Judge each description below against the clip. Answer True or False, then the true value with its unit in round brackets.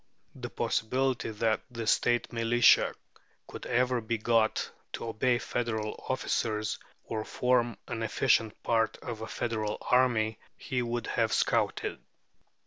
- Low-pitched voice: True (115 Hz)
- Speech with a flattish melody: True (1.8 semitones)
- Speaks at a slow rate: True (130 wpm)